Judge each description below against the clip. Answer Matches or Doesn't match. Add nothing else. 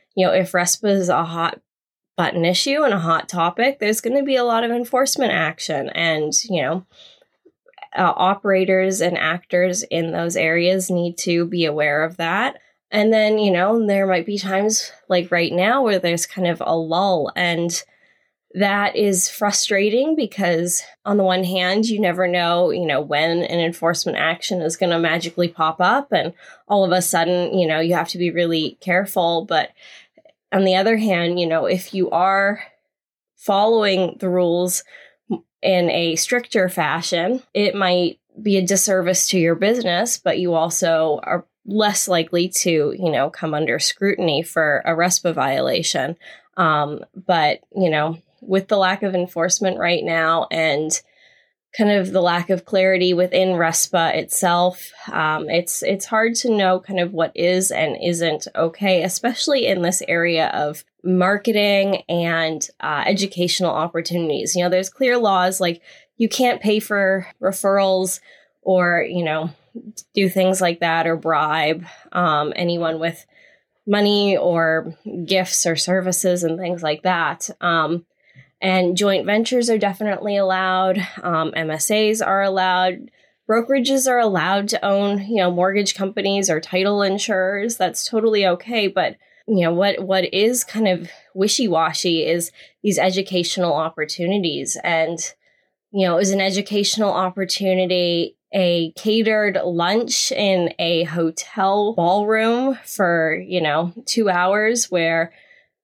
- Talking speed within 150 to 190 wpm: Matches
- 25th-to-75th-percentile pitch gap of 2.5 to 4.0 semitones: Matches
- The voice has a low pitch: Doesn't match